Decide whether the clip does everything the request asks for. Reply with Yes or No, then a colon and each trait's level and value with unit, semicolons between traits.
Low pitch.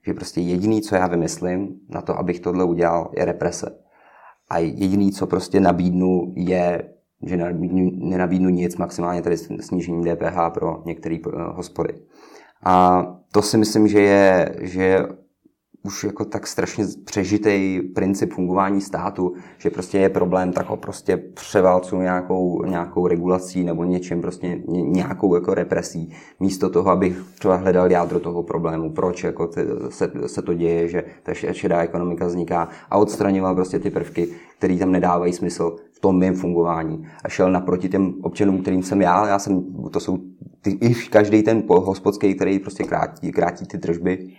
Yes: very low, 90 Hz